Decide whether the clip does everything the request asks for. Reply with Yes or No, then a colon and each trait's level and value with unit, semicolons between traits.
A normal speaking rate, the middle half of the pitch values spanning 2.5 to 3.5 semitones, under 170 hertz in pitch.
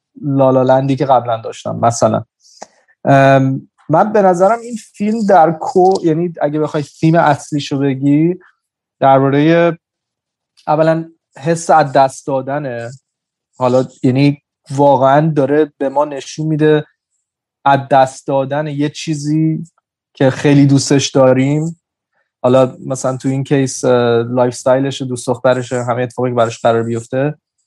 Yes: average, 120 wpm; average, 2.9 semitones; medium, 140 Hz